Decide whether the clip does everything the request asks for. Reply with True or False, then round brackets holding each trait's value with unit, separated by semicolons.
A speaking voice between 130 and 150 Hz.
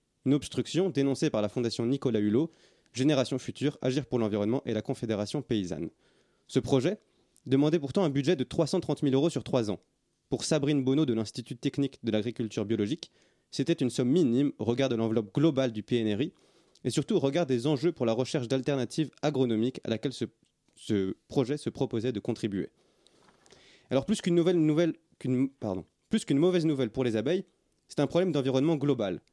True (135 Hz)